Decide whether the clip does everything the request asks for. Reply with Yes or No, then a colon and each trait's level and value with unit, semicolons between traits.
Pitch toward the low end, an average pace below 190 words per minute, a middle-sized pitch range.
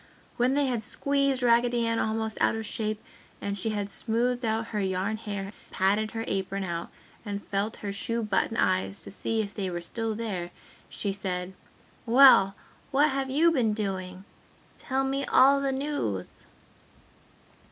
No: high, 220 Hz; average, 165 wpm; average, 3.9 semitones